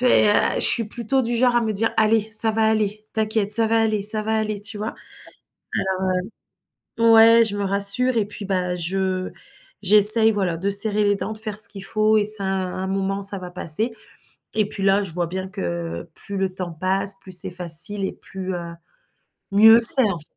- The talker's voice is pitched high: Yes, high, 205 Hz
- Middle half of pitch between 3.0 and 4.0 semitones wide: No, narrow, 2.5 semitones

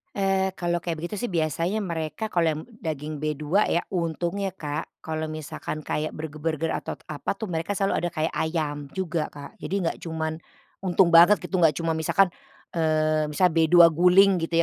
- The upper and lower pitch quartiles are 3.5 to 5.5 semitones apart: No, narrow, 2.6 semitones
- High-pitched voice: No, medium, 165 Hz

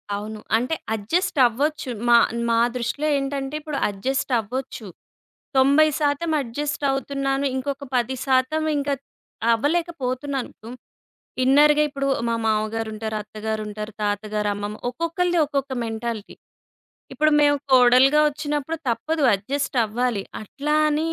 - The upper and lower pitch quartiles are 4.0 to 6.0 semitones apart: Yes, average, 4.5 semitones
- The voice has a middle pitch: No, very high, 265 Hz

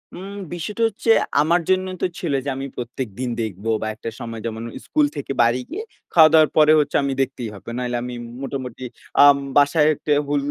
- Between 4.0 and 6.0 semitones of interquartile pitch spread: Yes, average, 4.7 semitones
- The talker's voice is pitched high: No, medium, 140 Hz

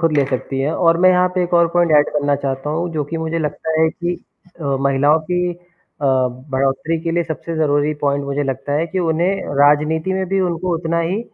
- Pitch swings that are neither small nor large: Yes, average, 3.2 semitones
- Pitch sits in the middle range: Yes, medium, 160 Hz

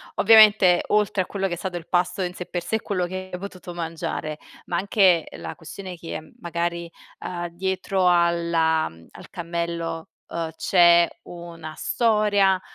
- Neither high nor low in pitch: Yes, medium, 175 Hz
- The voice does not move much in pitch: Yes, narrow, 2.0 semitones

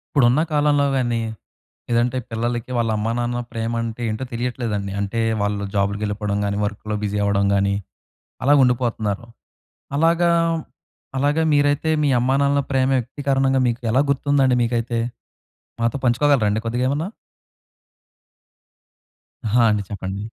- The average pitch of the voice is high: No, low, 120 Hz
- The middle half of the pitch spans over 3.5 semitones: Yes, average, 4.1 semitones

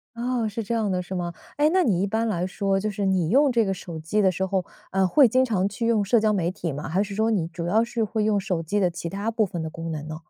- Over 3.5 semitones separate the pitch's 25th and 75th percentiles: Yes, average, 4.0 semitones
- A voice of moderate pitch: No, high, 195 Hz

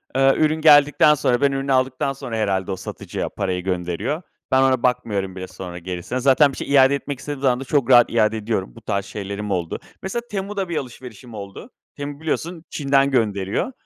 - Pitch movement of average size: No, wide, 6.0 semitones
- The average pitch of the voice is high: No, low, 130 Hz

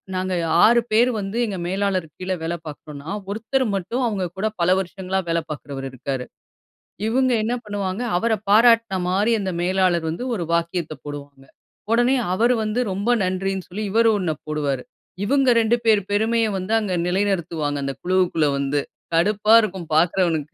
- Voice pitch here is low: No, high, 190 Hz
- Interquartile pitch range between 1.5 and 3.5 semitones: No, average, 4.5 semitones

